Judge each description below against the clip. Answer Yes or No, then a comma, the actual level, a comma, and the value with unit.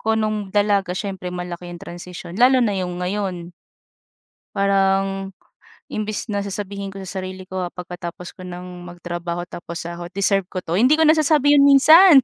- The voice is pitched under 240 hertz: Yes, high, 190 Hz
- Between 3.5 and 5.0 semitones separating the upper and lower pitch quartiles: No, average, 2.8 semitones